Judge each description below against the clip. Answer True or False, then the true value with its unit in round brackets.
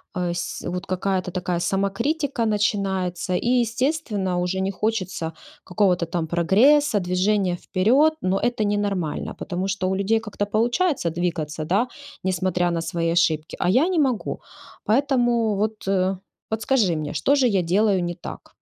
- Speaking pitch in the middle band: False (195 Hz)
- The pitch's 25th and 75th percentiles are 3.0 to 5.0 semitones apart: True (4.1 semitones)